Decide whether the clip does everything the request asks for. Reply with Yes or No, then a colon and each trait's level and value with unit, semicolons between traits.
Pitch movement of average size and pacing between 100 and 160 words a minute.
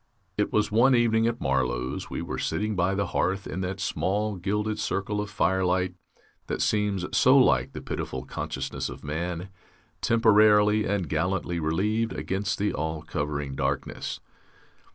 Yes: average, 3.9 semitones; average, 150 wpm